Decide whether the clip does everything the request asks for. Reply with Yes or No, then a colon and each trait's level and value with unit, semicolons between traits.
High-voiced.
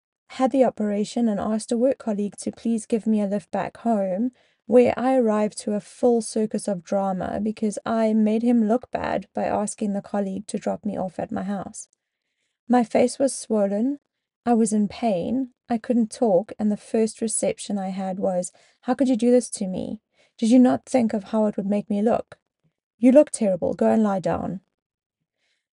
Yes: high, 225 Hz